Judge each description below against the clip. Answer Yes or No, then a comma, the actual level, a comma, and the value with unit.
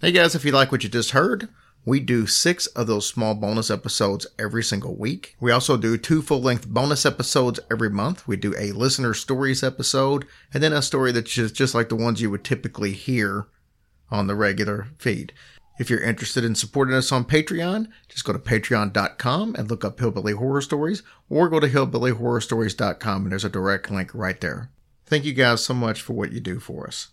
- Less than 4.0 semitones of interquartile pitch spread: No, average, 4.3 semitones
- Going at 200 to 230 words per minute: Yes, fast, 205 wpm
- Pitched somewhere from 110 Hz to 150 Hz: Yes, low, 120 Hz